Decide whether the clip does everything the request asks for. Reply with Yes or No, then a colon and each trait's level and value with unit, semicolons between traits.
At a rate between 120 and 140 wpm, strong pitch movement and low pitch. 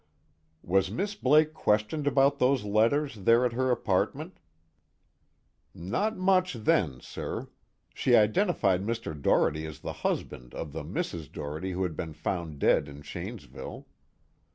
Yes: slow, 135 wpm; wide, 8.6 semitones; low, 105 Hz